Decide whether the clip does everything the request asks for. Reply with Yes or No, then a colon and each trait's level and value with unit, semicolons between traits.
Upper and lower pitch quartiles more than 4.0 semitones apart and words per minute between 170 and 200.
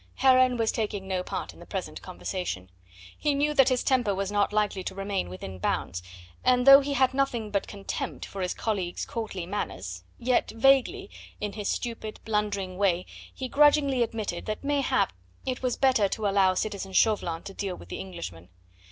Yes: average, 5.0 semitones; average, 180 wpm